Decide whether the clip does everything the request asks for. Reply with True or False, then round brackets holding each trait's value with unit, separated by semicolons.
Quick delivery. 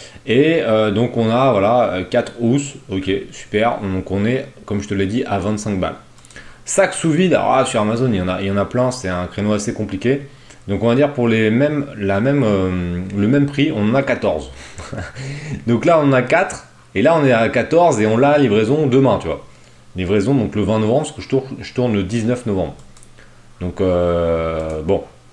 True (225 wpm)